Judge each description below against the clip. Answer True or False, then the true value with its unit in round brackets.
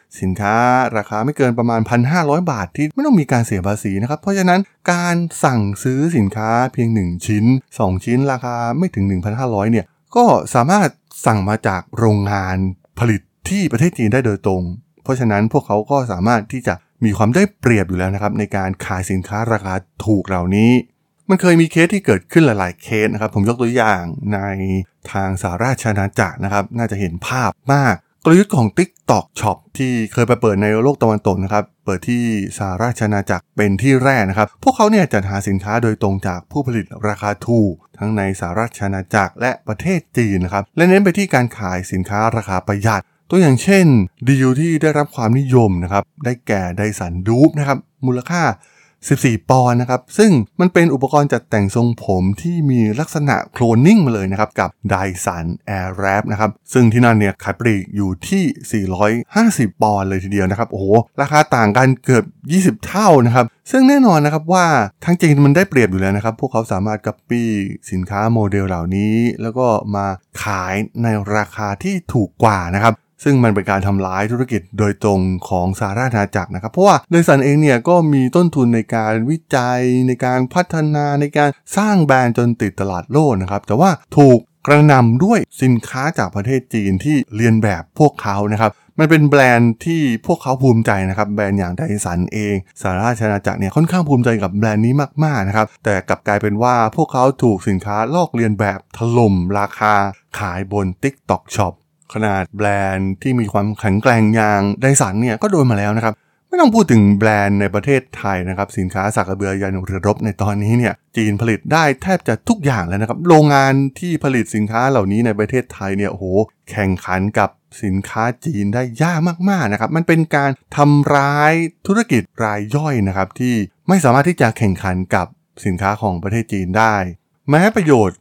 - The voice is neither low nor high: False (115 Hz)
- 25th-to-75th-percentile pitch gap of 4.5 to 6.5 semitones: True (5.5 semitones)